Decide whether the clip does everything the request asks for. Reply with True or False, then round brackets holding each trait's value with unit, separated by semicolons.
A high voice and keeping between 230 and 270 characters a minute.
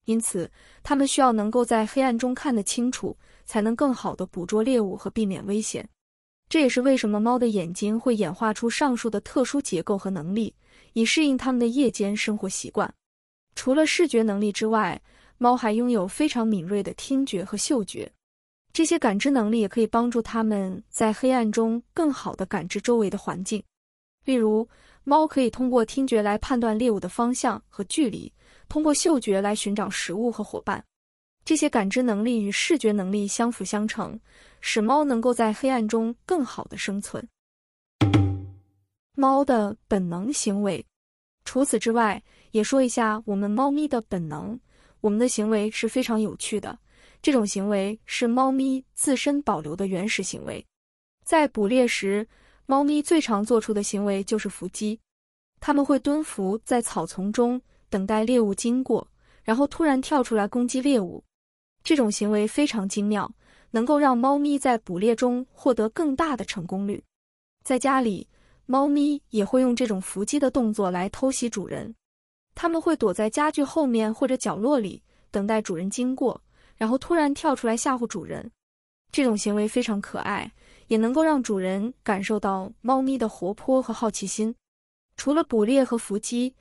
True (230 Hz; 260 characters per minute)